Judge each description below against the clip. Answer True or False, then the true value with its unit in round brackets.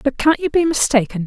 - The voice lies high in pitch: True (275 Hz)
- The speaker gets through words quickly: True (235 wpm)